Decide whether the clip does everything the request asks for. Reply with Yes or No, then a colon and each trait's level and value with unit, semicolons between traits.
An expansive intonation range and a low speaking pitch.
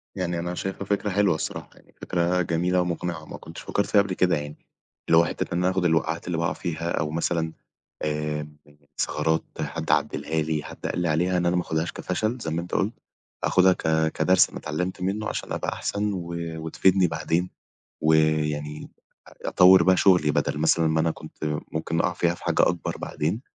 No: narrow, 2.5 semitones; very low, 85 Hz